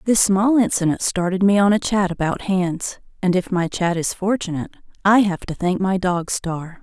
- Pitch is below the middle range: No, high, 190 Hz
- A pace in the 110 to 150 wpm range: No, average, 200 wpm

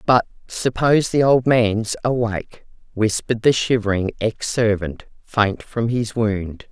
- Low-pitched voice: Yes, low, 110 Hz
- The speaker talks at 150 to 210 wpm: No, slow, 135 wpm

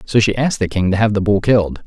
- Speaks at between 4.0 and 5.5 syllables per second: No, 6.8 syllables/s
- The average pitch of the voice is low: Yes, low, 100 Hz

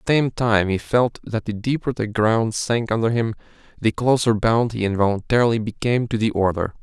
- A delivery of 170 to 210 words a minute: Yes, average, 200 wpm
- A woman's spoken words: No, male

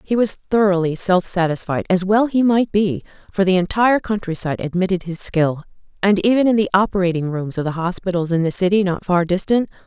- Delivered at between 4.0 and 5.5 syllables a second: No, 5.8 syllables/s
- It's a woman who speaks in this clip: Yes, female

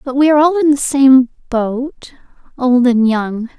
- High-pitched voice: Yes, very high, 260 Hz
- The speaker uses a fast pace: No, average, 185 wpm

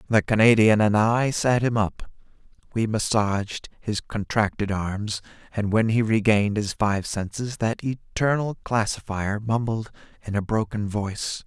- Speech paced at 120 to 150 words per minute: Yes, average, 140 wpm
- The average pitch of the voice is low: Yes, low, 110 Hz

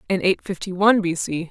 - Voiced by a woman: Yes, female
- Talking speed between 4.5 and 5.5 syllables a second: No, 6.0 syllables/s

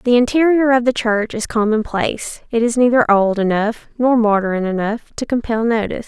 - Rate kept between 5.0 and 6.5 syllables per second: Yes, 5.1 syllables/s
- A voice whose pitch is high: Yes, high, 230 Hz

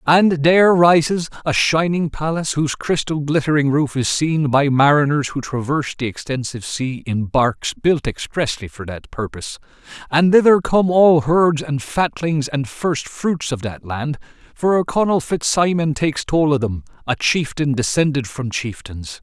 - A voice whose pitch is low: No, medium, 145 Hz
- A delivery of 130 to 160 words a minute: Yes, average, 155 wpm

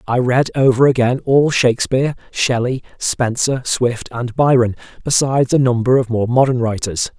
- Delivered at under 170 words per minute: Yes, average, 150 wpm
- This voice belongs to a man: Yes, male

